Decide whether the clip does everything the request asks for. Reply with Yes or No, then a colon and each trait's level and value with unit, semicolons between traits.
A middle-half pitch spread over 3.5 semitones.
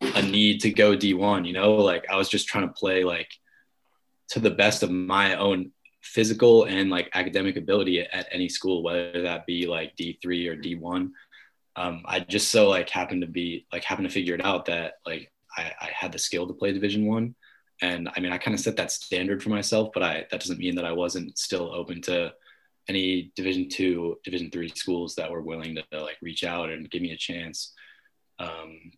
No: narrow, 2.4 semitones